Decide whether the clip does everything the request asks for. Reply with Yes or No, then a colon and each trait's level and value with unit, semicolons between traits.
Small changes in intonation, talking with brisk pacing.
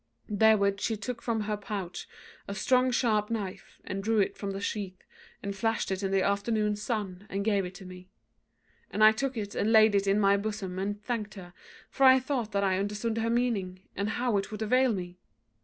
Yes: narrow, 2.2 semitones; fast, 210 wpm